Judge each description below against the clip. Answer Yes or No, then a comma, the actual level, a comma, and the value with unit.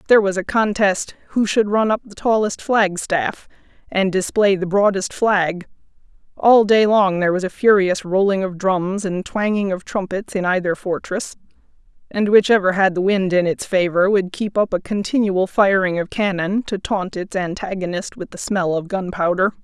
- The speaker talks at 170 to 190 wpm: Yes, average, 180 wpm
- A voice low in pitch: No, high, 195 Hz